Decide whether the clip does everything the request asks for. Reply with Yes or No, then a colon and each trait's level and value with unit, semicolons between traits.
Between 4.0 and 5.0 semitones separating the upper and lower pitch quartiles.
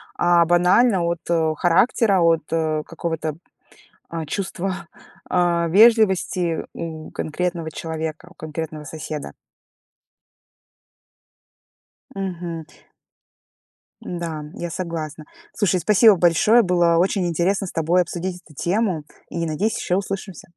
No: narrow, 2.6 semitones